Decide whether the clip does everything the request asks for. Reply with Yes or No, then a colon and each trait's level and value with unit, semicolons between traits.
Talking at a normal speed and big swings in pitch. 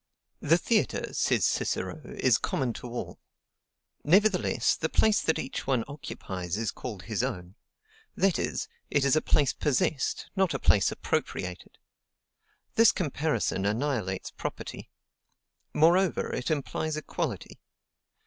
No: slow, 125 wpm; wide, 6.6 semitones